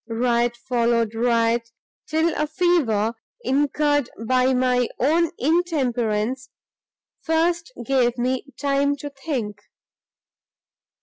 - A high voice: Yes, very high, 255 Hz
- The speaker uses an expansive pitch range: No, average, 4.1 semitones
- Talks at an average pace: No, slow, 95 wpm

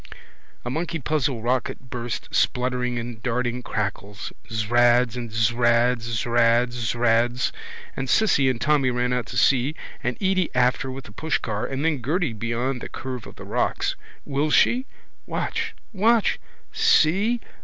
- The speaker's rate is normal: Yes, average, 150 wpm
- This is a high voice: No, low, 125 Hz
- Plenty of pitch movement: No, average, 3.1 semitones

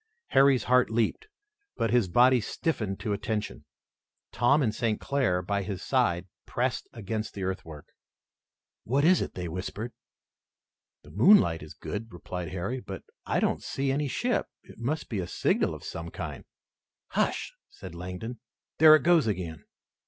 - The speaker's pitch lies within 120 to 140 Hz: No, low, 110 Hz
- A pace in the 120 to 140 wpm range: No, average, 155 wpm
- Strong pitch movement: Yes, wide, 6.2 semitones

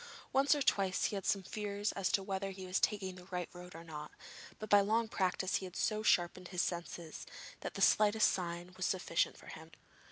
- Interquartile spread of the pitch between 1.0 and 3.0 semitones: Yes, narrow, 2.5 semitones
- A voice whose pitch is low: No, high, 190 Hz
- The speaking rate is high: Yes, fast, 220 wpm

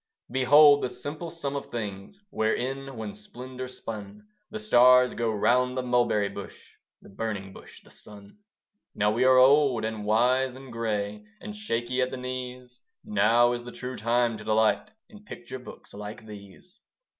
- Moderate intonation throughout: Yes, average, 3.3 semitones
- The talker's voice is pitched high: No, low, 120 Hz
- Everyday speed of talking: Yes, average, 170 wpm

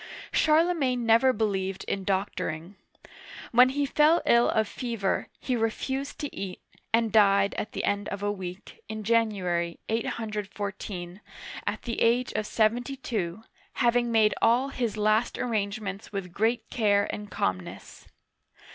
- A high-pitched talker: Yes, high, 215 Hz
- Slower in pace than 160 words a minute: Yes, average, 140 wpm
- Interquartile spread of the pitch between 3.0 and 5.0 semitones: Yes, average, 3.3 semitones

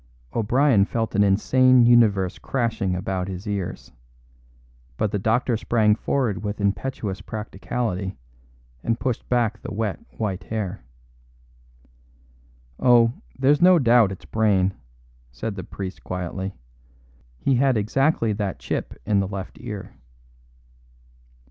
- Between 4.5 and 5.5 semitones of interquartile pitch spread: No, average, 3.7 semitones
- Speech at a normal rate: No, slow, 120 wpm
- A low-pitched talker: Yes, low, 105 Hz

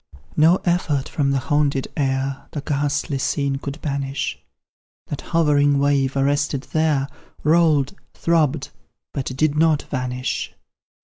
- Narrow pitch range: Yes, narrow, 1.9 semitones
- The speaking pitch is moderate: Yes, medium, 145 Hz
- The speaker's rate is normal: No, slow, 120 wpm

